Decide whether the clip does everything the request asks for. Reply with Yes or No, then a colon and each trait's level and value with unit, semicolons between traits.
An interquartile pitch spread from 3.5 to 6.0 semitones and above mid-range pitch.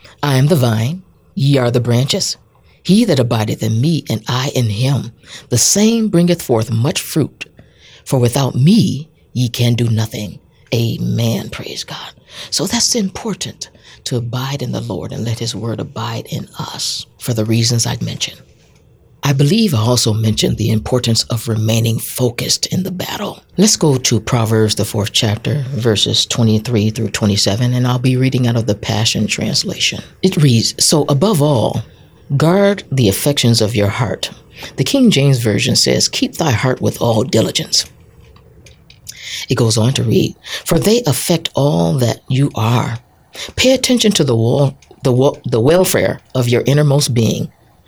No: average, 4.0 semitones; low, 125 Hz